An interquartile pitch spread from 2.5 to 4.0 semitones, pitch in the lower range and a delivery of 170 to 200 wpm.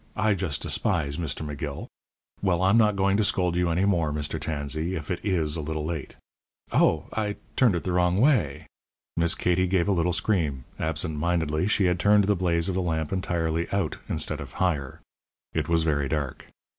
Yes: average, 3.3 semitones; very low, 85 Hz; average, 195 wpm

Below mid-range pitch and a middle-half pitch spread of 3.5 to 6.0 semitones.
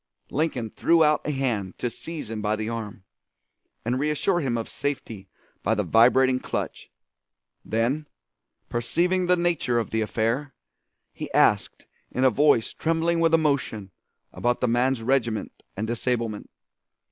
Yes: low, 125 Hz; average, 5.1 semitones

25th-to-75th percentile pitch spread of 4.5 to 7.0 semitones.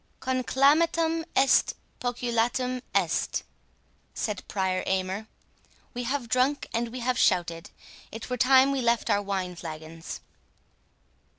Yes: wide, 5.4 semitones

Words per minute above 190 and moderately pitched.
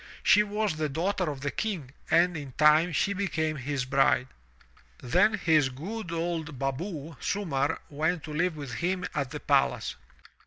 No: average, 160 wpm; medium, 160 Hz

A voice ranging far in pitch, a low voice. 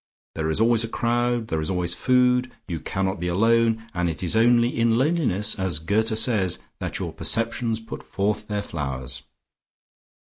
No: average, 4.6 semitones; low, 110 Hz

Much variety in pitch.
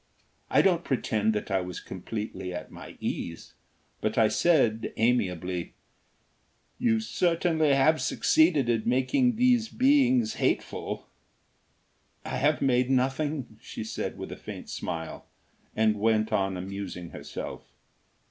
Yes: wide, 8.0 semitones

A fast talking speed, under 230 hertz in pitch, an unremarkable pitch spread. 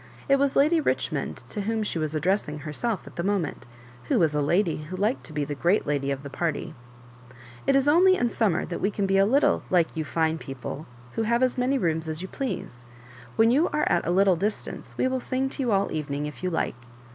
No: fast, 240 wpm; high, 190 Hz; wide, 7.3 semitones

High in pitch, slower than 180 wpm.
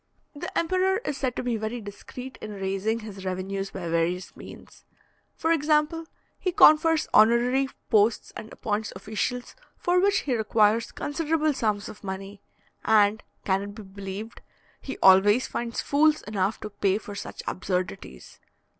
Yes: high, 220 Hz; average, 150 wpm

